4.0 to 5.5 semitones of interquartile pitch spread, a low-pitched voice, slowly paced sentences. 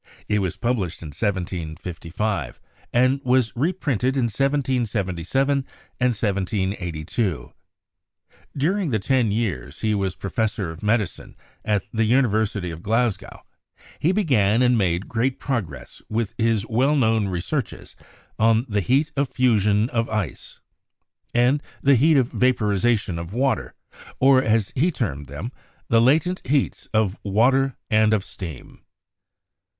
Yes: average, 4.7 semitones; low, 110 Hz; slow, 130 wpm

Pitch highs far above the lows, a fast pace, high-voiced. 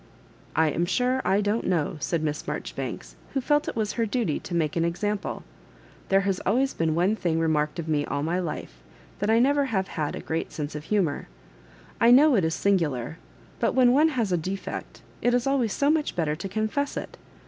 Yes: wide, 7.0 semitones; fast, 215 wpm; high, 195 Hz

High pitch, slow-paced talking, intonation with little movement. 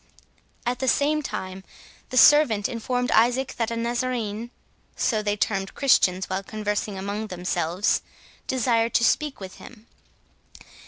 No: high, 225 Hz; slow, 130 wpm; average, 3.9 semitones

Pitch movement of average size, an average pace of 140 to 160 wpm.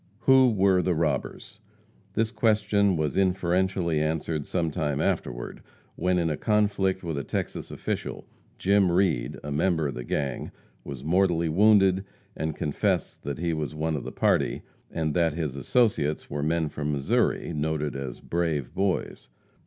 Yes: average, 4.2 semitones; average, 155 wpm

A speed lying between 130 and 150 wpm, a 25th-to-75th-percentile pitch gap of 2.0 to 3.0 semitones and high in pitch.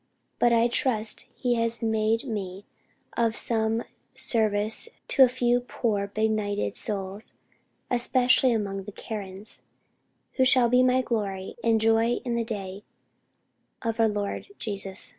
Yes: slow, 135 wpm; average, 2.7 semitones; high, 225 Hz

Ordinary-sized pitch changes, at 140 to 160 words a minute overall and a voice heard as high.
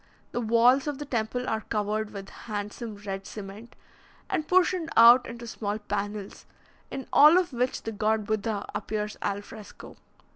Yes: average, 3.1 semitones; average, 155 wpm; high, 220 Hz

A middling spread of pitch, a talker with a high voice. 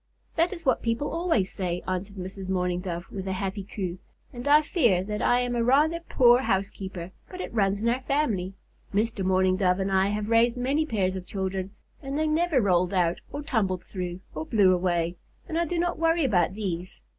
No: wide, 5.9 semitones; high, 200 Hz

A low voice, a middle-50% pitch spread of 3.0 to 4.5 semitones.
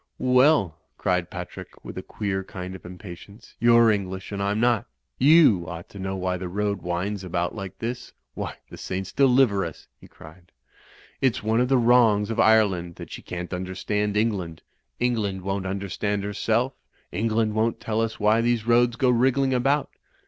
Yes: low, 105 Hz; average, 4.0 semitones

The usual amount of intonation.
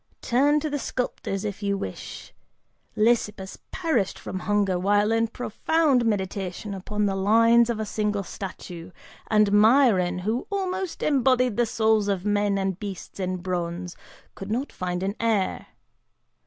Yes: average, 3.6 semitones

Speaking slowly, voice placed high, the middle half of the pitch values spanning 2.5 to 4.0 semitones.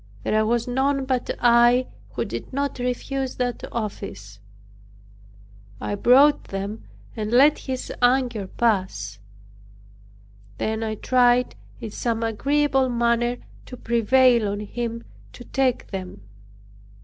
Yes: slow, 115 wpm; high, 240 Hz; average, 2.9 semitones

